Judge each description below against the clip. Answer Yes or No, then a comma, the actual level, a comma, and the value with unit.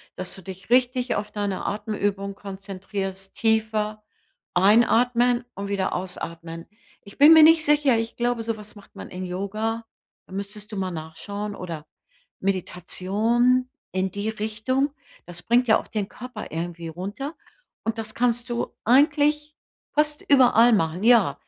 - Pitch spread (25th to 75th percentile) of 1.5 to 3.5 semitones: No, average, 4.0 semitones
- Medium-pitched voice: No, high, 215 Hz